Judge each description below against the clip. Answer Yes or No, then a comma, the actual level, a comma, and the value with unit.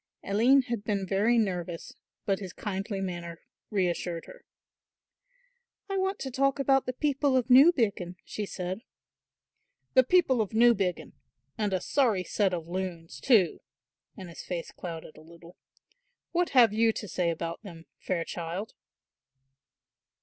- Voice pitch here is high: Yes, high, 200 Hz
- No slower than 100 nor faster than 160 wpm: Yes, average, 140 wpm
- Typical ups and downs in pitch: No, wide, 6.0 semitones